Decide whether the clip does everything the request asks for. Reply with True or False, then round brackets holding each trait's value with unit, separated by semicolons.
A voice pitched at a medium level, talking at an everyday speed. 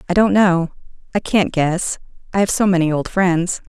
True (180 Hz; 160 wpm)